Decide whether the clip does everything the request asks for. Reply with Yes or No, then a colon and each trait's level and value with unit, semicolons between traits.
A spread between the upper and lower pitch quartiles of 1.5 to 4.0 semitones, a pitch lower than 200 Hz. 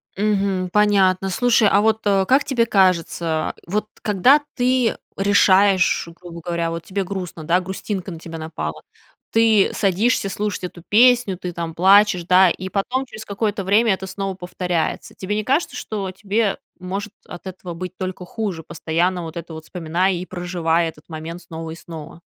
Yes: average, 3.3 semitones; high, 190 Hz